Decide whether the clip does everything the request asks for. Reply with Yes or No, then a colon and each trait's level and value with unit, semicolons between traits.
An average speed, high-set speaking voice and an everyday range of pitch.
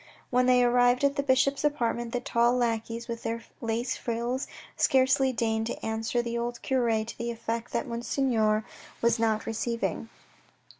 No: average, 160 wpm; high, 235 Hz; narrow, 1.6 semitones